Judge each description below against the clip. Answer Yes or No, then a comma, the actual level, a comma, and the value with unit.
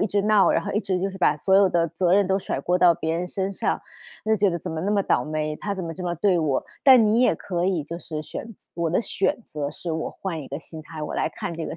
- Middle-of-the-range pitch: Yes, medium, 175 Hz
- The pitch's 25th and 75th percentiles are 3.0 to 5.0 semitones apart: Yes, average, 3.7 semitones